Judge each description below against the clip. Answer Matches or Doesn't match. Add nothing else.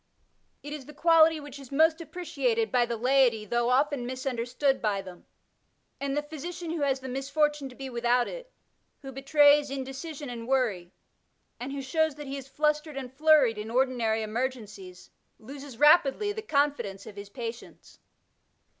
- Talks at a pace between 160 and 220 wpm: Matches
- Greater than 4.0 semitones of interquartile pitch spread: Doesn't match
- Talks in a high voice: Matches